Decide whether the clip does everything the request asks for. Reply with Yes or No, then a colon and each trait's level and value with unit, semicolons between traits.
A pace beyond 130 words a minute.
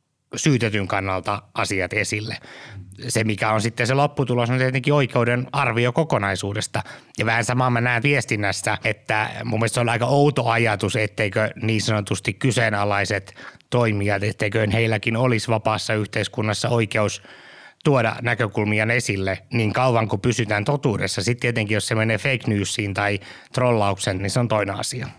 Yes: average, 150 wpm